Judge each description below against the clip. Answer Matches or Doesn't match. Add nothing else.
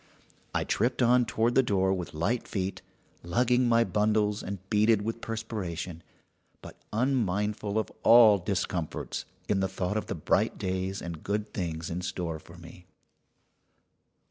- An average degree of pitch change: Matches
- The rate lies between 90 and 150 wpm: Matches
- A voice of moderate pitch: Doesn't match